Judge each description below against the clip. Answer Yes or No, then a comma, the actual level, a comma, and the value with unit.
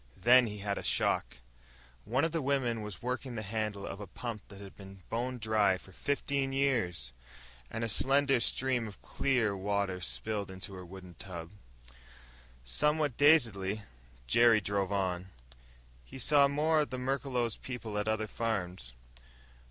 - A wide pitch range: No, average, 4.9 semitones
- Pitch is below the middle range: Yes, low, 110 Hz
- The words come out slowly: No, average, 155 wpm